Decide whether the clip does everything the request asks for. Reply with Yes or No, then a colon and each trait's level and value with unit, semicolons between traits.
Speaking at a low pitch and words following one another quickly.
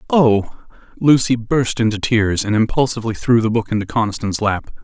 No: low, 115 Hz; average, 160 wpm